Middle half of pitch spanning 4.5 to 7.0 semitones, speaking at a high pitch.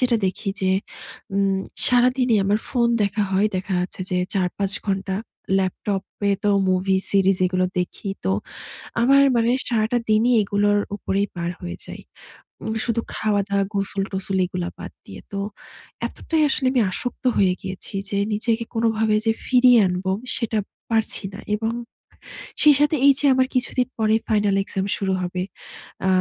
No: average, 3.3 semitones; high, 205 Hz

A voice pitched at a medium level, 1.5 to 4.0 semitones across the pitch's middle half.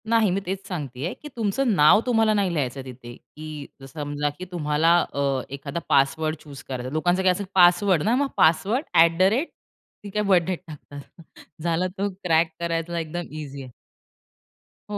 No: medium, 165 Hz; average, 4.6 semitones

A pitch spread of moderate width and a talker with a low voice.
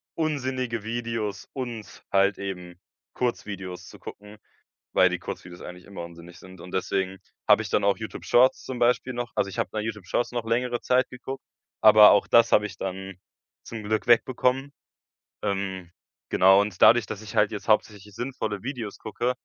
Yes: average, 3.9 semitones; low, 105 Hz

